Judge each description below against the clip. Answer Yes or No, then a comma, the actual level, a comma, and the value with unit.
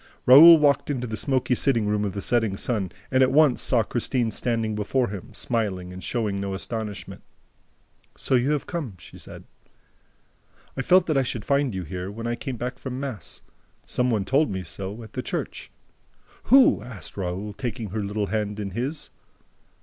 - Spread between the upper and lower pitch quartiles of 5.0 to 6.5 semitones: No, average, 4.4 semitones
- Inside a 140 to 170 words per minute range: No, average, 185 wpm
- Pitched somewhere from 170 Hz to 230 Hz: No, low, 115 Hz